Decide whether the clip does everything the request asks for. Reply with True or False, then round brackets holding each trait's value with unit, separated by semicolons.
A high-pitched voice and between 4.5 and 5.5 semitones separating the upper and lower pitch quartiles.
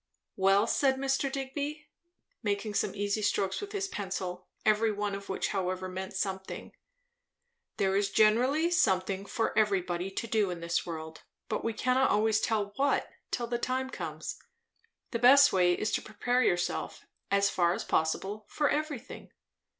True (210 Hz; 4.9 semitones)